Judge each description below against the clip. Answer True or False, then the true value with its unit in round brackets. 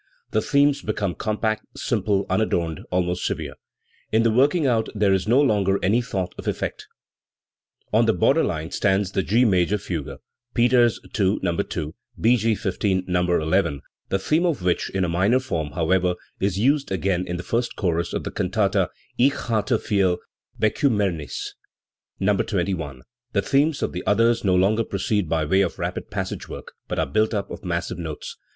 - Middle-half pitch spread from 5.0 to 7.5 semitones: False (4.3 semitones)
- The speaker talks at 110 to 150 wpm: False (175 wpm)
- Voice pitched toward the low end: True (100 Hz)